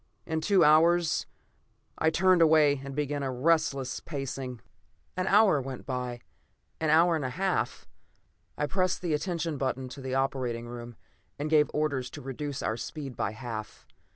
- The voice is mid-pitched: Yes, medium, 145 Hz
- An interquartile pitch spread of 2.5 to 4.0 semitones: Yes, average, 3.7 semitones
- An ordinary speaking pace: Yes, average, 160 wpm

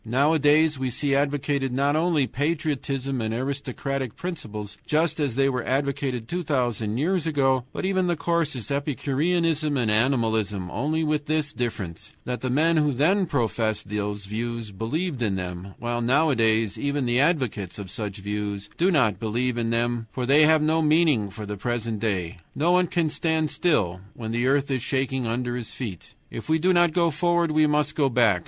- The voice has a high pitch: No, low, 135 Hz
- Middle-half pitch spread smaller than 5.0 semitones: No, average, 5.3 semitones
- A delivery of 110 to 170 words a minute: No, average, 180 wpm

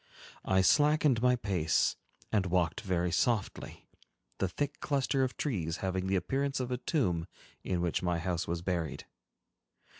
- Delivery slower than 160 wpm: Yes, average, 150 wpm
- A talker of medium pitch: No, very low, 95 Hz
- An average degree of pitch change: No, wide, 6.5 semitones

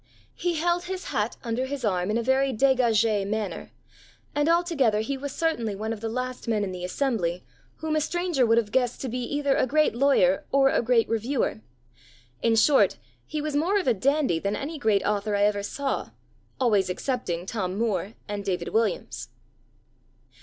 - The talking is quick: No, average, 185 wpm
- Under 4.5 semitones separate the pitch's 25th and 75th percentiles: No, average, 5.1 semitones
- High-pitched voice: Yes, high, 235 Hz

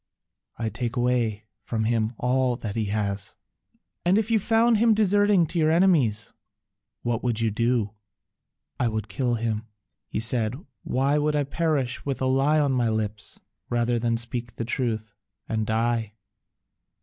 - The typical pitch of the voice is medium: No, low, 120 Hz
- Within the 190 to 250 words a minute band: No, average, 160 wpm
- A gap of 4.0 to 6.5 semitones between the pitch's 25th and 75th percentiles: Yes, average, 4.4 semitones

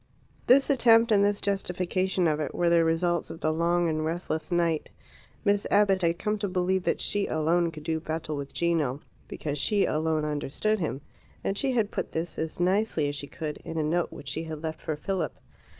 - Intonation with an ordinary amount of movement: Yes, average, 3.7 semitones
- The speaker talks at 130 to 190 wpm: No, fast, 205 wpm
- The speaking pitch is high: No, medium, 170 Hz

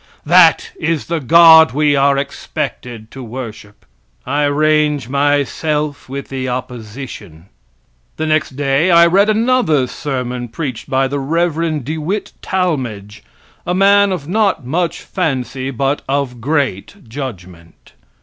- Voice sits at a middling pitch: Yes, medium, 145 Hz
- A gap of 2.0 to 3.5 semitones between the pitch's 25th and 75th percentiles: No, average, 4.1 semitones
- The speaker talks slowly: Yes, slow, 130 wpm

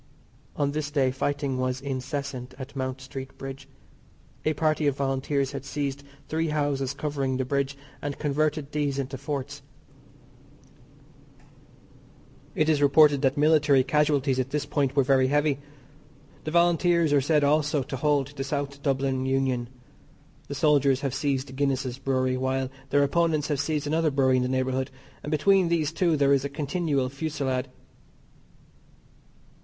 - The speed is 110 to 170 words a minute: Yes, average, 150 wpm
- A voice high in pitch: No, medium, 140 Hz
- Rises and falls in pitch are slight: Yes, narrow, 2.0 semitones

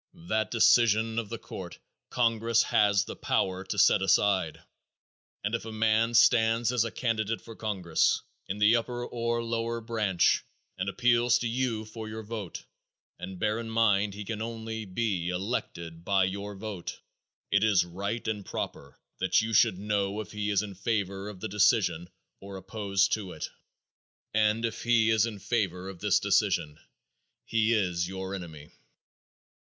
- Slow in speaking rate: No, average, 165 wpm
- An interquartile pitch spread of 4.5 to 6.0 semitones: No, average, 2.8 semitones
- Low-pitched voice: Yes, low, 105 Hz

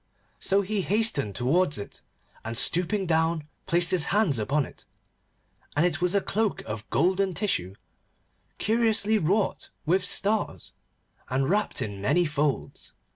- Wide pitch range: Yes, wide, 6.3 semitones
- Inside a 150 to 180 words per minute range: No, slow, 135 wpm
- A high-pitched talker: No, medium, 175 Hz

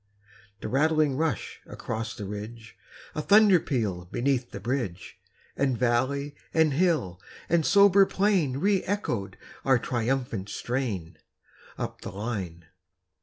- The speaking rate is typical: No, slow, 120 wpm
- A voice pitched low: Yes, low, 130 Hz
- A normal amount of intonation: No, wide, 6.6 semitones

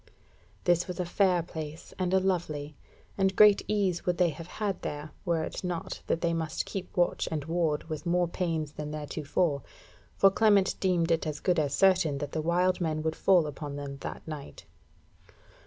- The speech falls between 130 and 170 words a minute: No, average, 190 wpm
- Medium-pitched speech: Yes, medium, 170 Hz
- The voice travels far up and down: No, average, 3.0 semitones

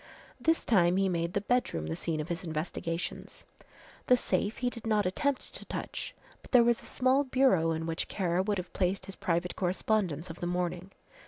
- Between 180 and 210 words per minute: Yes, average, 195 wpm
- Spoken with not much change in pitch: No, average, 4.9 semitones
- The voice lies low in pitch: No, medium, 185 Hz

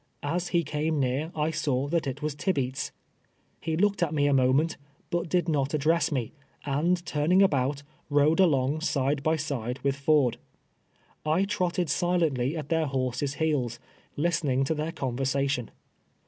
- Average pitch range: Yes, average, 3.2 semitones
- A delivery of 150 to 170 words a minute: Yes, average, 155 wpm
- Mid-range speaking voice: Yes, medium, 150 Hz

